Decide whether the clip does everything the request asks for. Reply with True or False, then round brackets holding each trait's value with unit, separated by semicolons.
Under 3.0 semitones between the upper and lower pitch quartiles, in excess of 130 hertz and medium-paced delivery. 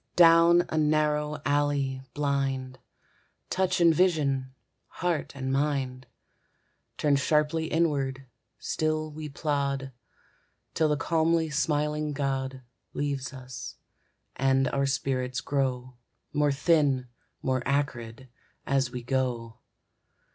False (2.4 semitones; 140 Hz; 105 wpm)